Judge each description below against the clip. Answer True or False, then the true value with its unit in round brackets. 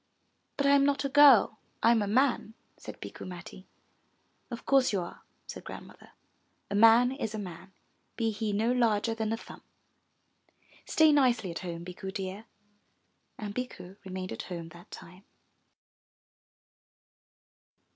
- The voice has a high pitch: True (215 Hz)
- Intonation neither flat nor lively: True (4.8 semitones)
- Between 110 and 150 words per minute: True (145 wpm)